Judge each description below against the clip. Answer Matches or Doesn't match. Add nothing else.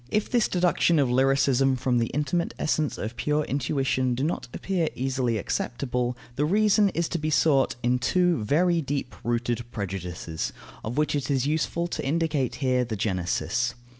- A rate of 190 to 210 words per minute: Doesn't match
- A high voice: Doesn't match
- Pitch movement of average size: Matches